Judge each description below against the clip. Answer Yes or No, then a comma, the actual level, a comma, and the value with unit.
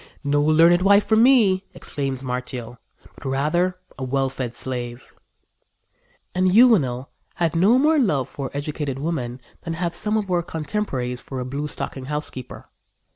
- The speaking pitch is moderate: Yes, medium, 150 Hz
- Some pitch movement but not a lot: No, wide, 5.8 semitones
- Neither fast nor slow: Yes, average, 150 wpm